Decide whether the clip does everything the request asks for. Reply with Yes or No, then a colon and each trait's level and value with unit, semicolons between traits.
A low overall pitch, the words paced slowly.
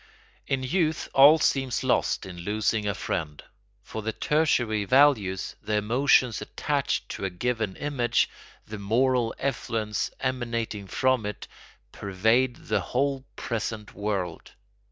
Yes: low, 115 Hz; slow, 125 wpm